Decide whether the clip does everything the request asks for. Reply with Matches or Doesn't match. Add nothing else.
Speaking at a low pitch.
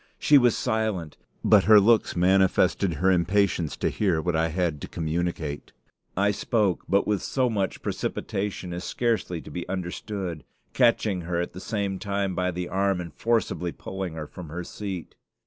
Matches